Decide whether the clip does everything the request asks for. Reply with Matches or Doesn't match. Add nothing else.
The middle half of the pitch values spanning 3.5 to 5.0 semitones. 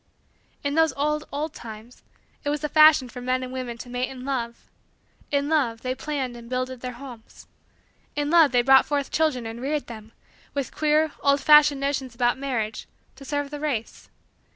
Doesn't match